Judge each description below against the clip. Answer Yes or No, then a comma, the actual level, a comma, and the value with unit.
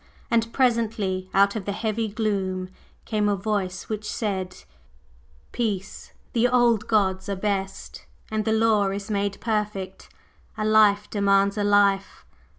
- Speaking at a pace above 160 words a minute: No, average, 140 wpm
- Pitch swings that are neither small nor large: No, narrow, 1.9 semitones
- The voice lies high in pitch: Yes, high, 205 Hz